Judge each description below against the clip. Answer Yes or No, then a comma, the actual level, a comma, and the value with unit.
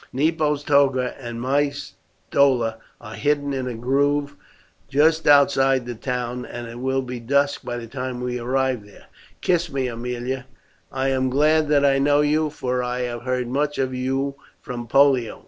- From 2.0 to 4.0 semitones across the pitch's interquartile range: Yes, narrow, 2.5 semitones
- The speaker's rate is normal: Yes, average, 170 wpm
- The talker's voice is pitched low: Yes, low, 130 Hz